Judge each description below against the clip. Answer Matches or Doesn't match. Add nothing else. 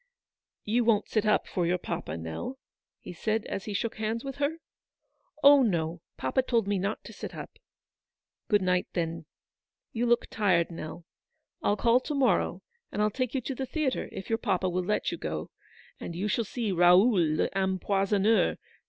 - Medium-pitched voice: Doesn't match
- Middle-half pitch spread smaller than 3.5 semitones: Doesn't match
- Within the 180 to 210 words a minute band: Matches